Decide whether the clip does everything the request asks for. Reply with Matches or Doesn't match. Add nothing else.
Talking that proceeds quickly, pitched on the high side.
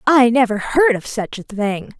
Matches